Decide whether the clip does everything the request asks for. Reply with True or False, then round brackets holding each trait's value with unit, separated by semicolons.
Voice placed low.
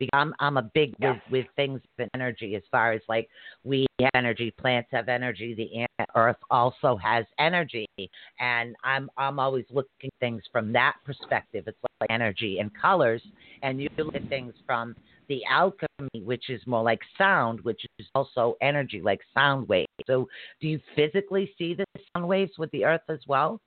True (130 Hz)